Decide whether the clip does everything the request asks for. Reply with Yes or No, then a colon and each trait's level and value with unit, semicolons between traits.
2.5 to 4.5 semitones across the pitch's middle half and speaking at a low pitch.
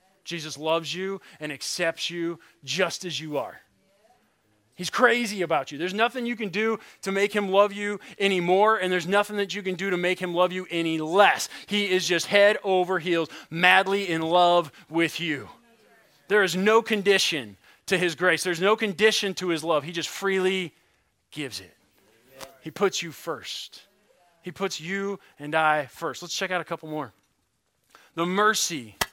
No: average, 3.4 semitones; medium, 180 Hz